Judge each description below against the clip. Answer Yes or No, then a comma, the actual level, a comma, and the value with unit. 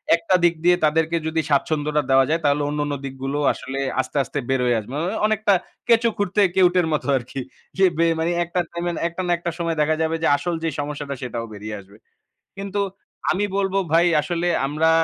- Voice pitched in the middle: Yes, medium, 160 Hz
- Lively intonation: No, average, 3.6 semitones